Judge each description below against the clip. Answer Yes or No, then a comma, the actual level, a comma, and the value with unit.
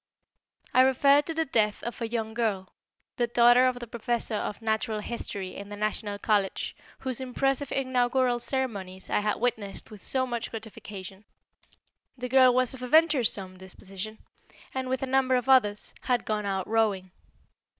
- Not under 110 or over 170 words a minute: Yes, average, 165 wpm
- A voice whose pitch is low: No, high, 235 Hz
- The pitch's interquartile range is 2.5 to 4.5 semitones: Yes, average, 3.6 semitones